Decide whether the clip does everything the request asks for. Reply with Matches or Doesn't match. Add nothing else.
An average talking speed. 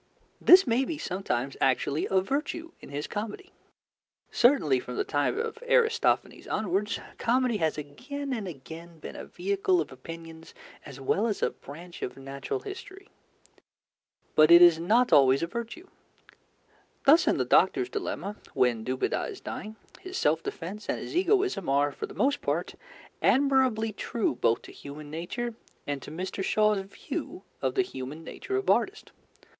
Matches